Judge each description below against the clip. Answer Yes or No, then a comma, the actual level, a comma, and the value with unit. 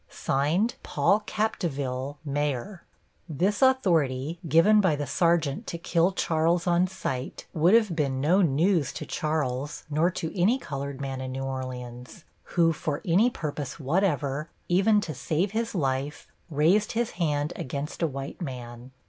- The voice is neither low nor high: Yes, medium, 155 Hz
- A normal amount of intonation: Yes, average, 4.7 semitones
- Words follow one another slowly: No, average, 145 wpm